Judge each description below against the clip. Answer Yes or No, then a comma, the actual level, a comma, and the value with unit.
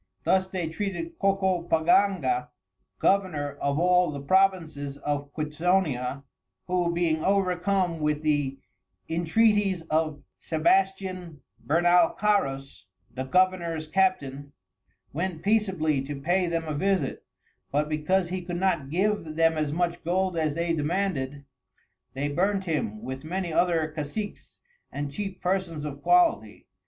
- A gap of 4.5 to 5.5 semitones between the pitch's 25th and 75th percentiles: No, average, 4.1 semitones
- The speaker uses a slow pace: Yes, slow, 125 wpm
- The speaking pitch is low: No, medium, 170 Hz